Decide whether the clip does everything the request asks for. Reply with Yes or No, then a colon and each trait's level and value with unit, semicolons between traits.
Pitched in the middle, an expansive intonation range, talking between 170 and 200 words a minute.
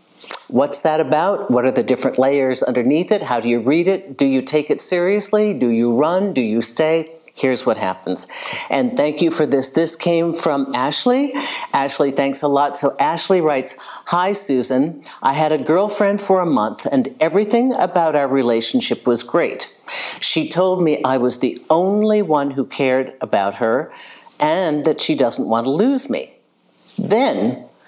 Yes: medium, 155 Hz; wide, 6.0 semitones; average, 175 wpm